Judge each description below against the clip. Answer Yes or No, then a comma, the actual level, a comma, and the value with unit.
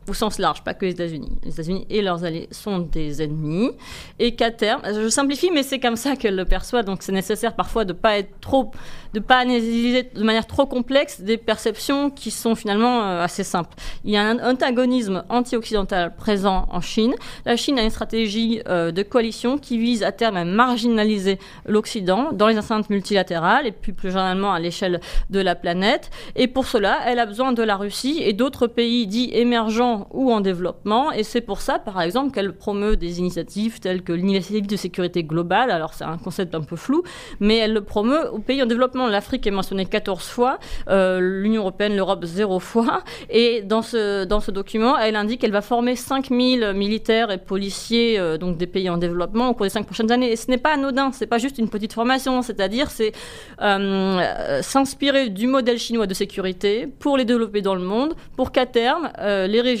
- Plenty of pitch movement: No, average, 4.0 semitones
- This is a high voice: Yes, high, 220 Hz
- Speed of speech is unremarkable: Yes, average, 205 wpm